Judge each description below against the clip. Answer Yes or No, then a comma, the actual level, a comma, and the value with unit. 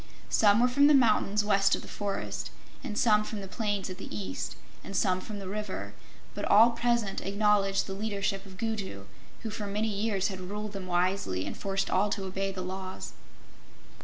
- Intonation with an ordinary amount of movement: No, narrow, 1.8 semitones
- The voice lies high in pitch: Yes, high, 200 Hz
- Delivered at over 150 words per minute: Yes, average, 190 wpm